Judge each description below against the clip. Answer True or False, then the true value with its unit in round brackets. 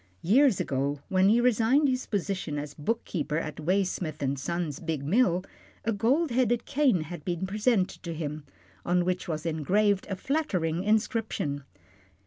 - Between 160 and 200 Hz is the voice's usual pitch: True (185 Hz)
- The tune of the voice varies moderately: False (6.2 semitones)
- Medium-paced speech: True (150 wpm)